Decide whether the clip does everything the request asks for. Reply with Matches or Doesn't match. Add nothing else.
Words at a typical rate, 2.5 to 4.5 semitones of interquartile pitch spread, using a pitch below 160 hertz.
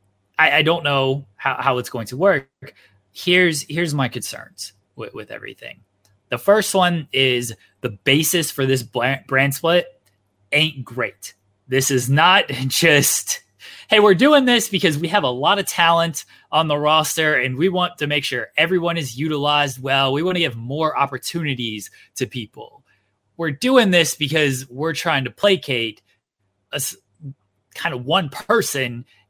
Doesn't match